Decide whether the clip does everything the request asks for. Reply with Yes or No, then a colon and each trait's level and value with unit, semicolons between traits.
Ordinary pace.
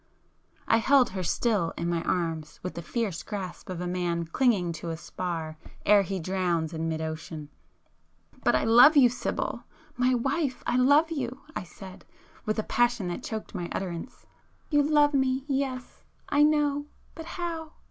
Yes: average, 170 wpm